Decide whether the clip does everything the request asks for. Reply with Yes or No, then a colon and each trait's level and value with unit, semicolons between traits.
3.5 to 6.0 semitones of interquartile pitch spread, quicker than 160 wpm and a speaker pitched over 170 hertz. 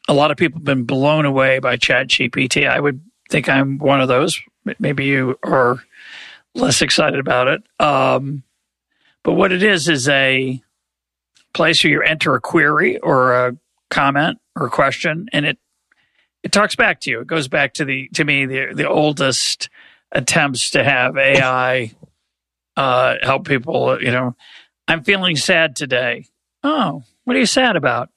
No: average, 3.9 semitones; average, 170 wpm; low, 135 Hz